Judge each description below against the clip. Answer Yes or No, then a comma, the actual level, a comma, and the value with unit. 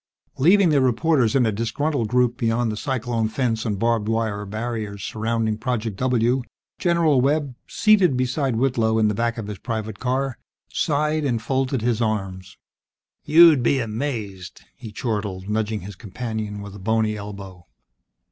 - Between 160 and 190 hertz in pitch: No, low, 115 Hz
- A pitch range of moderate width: Yes, average, 3.5 semitones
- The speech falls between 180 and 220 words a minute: No, average, 155 wpm